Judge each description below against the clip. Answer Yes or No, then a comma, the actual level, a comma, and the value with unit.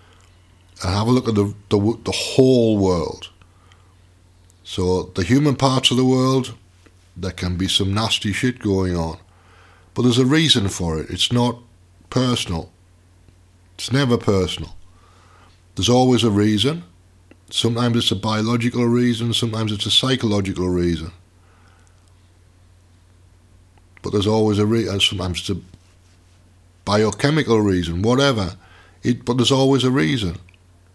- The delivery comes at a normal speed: No, slow, 130 wpm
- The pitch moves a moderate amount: Yes, average, 4.5 semitones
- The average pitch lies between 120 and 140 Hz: No, very low, 95 Hz